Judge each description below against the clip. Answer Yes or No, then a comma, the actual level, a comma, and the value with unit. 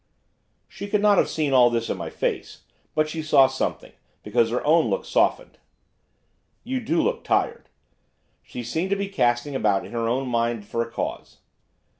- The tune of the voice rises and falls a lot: Yes, wide, 5.9 semitones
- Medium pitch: No, low, 130 Hz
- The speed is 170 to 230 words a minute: Yes, average, 180 wpm